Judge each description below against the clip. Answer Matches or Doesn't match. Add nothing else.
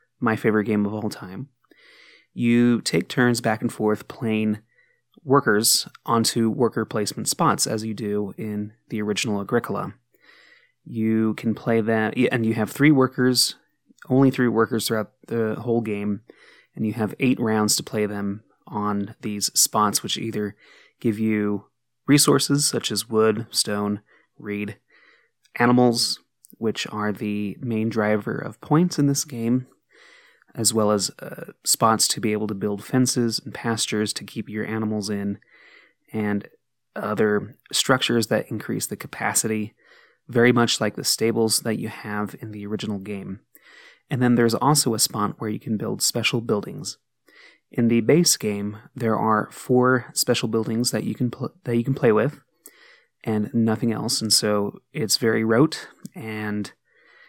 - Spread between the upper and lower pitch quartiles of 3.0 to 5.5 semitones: Doesn't match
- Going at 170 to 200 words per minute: Doesn't match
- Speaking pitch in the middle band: Doesn't match